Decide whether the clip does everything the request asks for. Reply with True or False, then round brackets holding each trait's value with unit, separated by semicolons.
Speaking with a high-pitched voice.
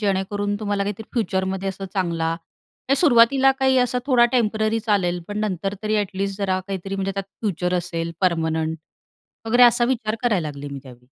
True (195 Hz)